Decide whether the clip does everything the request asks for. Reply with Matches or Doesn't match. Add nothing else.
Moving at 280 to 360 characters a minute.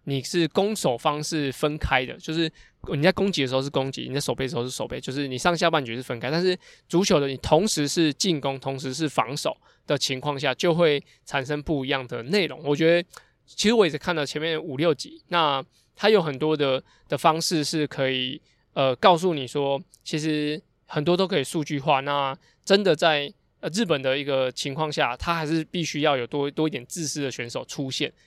Matches